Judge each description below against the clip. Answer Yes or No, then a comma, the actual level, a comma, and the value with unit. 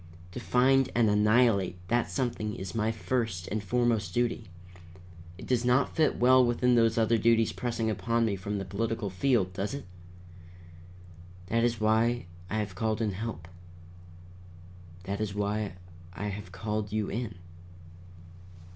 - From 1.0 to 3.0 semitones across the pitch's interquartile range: Yes, average, 2.7 semitones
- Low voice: Yes, low, 110 Hz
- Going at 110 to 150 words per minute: Yes, average, 145 wpm